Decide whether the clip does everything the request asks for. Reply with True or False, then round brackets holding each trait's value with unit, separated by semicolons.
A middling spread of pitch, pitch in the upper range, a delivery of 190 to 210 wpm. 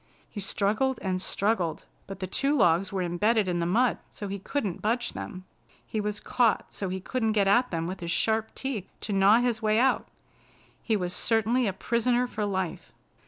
True (3.8 semitones; 210 Hz; 195 wpm)